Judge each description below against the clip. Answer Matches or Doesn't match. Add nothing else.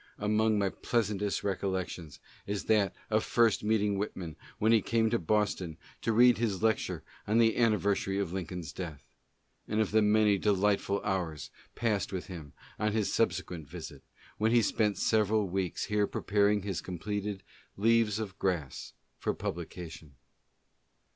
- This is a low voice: Matches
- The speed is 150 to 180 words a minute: Matches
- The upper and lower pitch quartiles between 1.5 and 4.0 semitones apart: Matches